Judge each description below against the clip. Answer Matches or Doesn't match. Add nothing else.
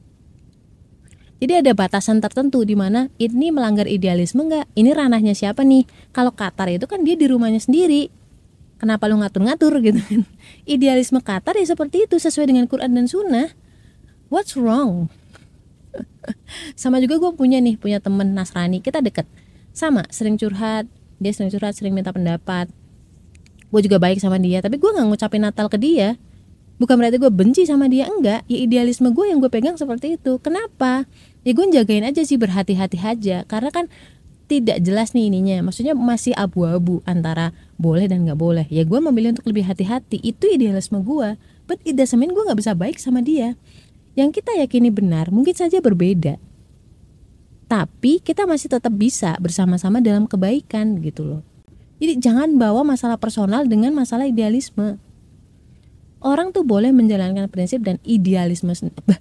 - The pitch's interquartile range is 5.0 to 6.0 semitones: Matches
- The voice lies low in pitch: Doesn't match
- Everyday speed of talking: Doesn't match